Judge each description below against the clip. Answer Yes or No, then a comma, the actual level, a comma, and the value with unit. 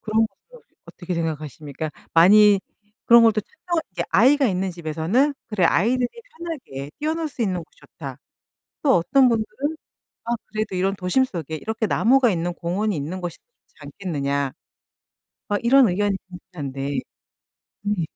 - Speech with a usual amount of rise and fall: No, wide, 6.4 semitones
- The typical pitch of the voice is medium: No, high, 200 Hz